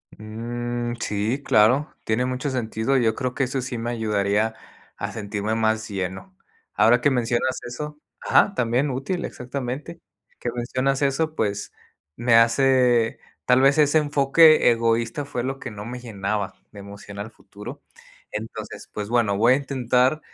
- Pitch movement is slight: No, average, 3.4 semitones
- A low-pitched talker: Yes, low, 120 Hz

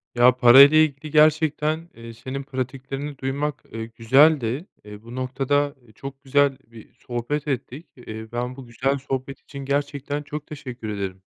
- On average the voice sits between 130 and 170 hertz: Yes, low, 135 Hz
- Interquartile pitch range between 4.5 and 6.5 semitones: No, average, 3.1 semitones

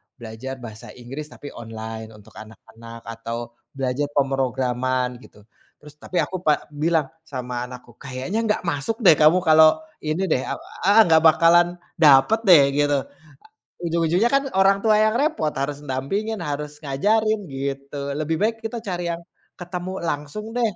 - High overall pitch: No, medium, 150 Hz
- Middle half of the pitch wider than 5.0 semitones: Yes, wide, 5.5 semitones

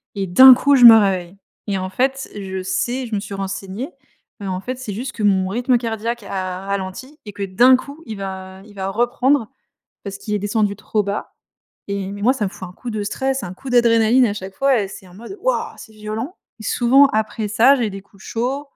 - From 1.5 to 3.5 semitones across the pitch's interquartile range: No, average, 4.2 semitones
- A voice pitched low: No, high, 215 Hz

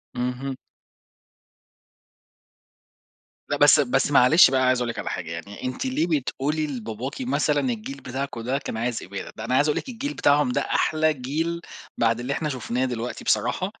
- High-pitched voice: No, low, 130 Hz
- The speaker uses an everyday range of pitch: Yes, average, 3.8 semitones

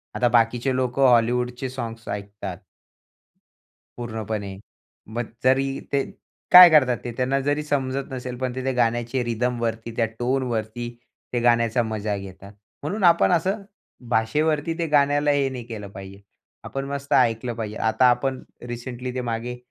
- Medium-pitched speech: No, low, 125 Hz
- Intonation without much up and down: No, average, 3.0 semitones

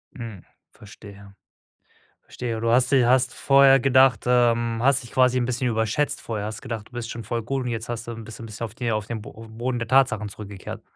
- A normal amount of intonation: No, narrow, 2.2 semitones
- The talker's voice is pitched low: Yes, low, 115 Hz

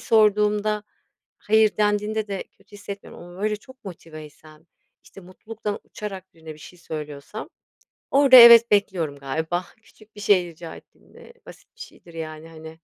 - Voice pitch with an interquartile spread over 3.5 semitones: Yes, average, 4.8 semitones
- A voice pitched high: Yes, high, 195 Hz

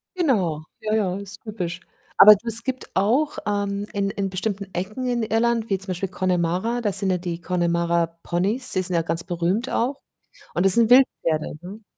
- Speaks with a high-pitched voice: Yes, high, 195 Hz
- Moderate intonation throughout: Yes, average, 4.1 semitones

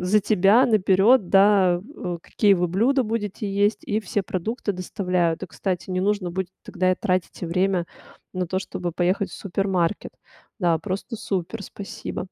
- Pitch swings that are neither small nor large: No, narrow, 2.3 semitones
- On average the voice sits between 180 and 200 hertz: Yes, high, 190 Hz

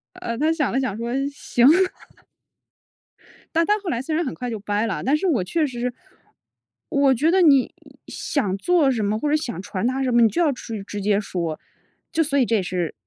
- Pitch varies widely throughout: Yes, wide, 6.2 semitones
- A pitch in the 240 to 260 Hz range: Yes, very high, 250 Hz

